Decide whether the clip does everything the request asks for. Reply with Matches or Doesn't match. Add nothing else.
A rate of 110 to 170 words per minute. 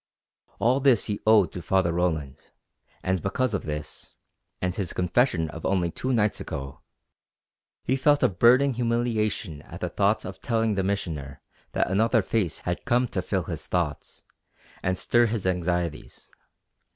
Matches